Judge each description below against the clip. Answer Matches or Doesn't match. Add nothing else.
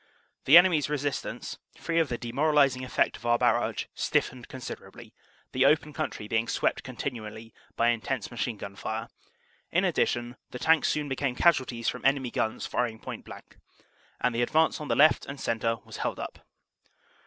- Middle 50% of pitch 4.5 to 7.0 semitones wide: Doesn't match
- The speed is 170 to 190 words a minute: Matches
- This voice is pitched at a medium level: Doesn't match